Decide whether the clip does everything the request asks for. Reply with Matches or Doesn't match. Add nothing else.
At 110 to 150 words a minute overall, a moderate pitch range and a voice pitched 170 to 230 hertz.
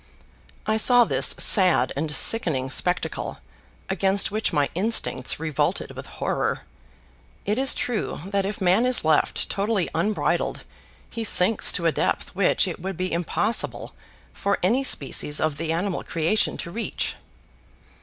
Matches